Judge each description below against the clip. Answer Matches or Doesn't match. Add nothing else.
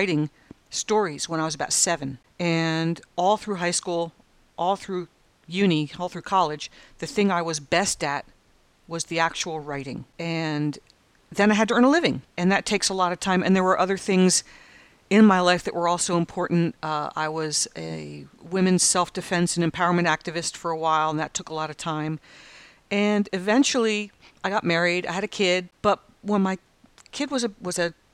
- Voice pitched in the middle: Matches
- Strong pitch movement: Doesn't match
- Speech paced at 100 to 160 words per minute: Doesn't match